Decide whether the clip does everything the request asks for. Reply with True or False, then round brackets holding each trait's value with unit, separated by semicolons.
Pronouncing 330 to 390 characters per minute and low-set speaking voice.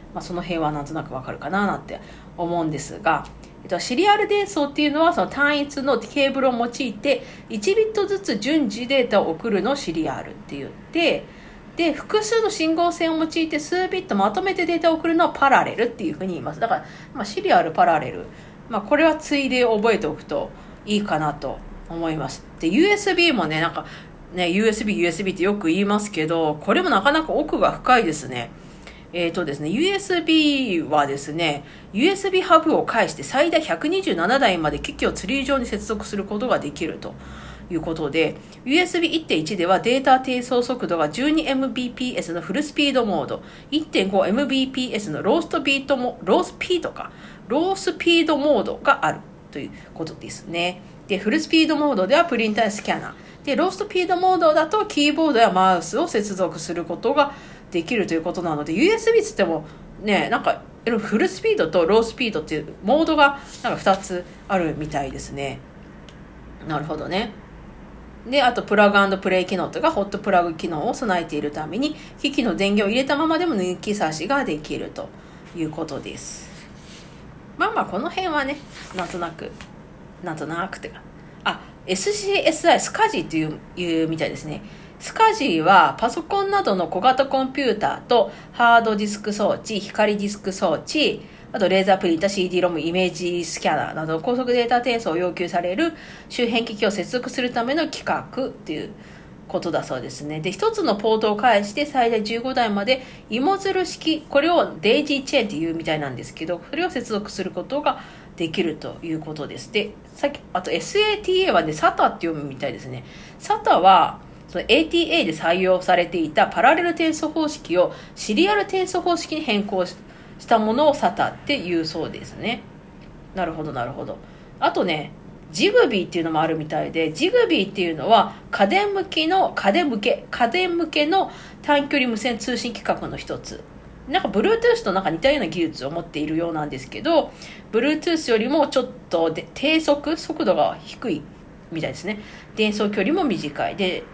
False (375 characters per minute; 225 Hz)